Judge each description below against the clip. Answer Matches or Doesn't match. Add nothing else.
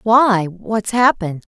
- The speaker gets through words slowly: Matches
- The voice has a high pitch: Matches